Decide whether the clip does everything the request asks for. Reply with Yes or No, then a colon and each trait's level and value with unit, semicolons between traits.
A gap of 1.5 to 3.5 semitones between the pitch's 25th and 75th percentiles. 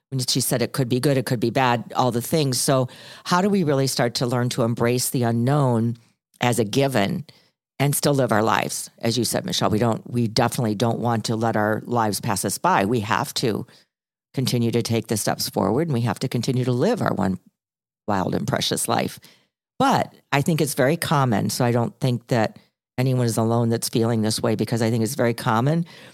Yes: narrow, 2.6 semitones